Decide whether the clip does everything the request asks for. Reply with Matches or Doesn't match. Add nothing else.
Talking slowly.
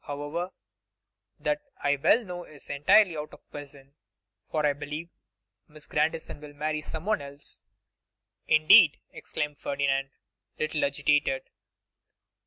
Matches